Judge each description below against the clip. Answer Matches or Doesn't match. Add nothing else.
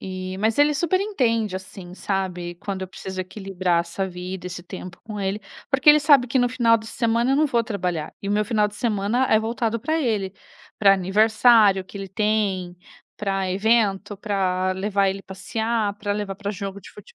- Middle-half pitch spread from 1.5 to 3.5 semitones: Matches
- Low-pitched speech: Doesn't match